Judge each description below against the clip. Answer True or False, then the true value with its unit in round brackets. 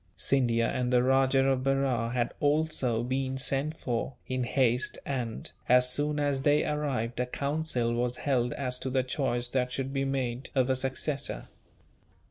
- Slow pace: False (165 wpm)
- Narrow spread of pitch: True (1.8 semitones)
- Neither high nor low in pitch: False (130 Hz)